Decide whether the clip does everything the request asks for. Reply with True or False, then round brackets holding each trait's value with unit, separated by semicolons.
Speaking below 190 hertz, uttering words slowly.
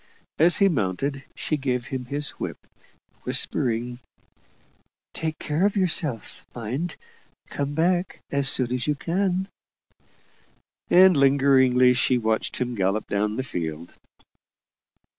True (135 Hz; 120 wpm)